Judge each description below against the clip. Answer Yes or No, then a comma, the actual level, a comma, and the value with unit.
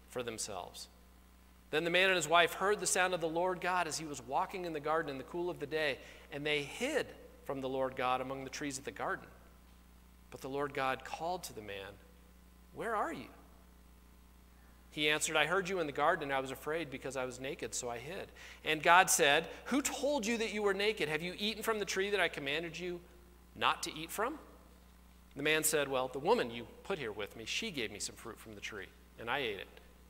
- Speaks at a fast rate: Yes, fast, 235 wpm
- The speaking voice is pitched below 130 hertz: No, medium, 140 Hz